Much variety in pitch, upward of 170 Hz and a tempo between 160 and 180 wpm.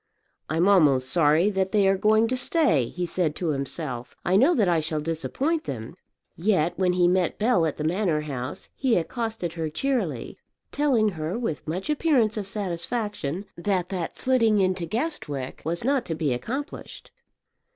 Yes: wide, 5.9 semitones; medium, 185 Hz; average, 170 wpm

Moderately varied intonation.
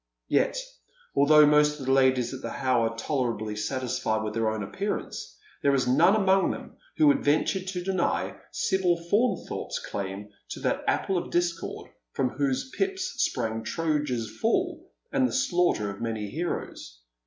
No: wide, 8.5 semitones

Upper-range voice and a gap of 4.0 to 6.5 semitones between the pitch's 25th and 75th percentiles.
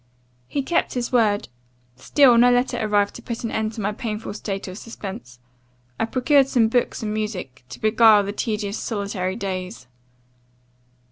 No: high, 215 Hz; average, 2.9 semitones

